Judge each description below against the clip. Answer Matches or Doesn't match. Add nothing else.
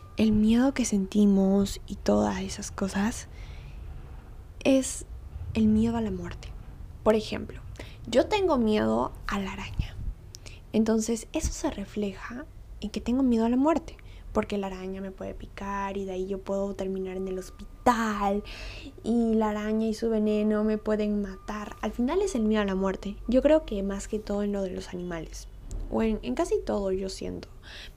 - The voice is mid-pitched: Doesn't match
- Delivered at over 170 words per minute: Matches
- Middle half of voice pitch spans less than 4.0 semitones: Matches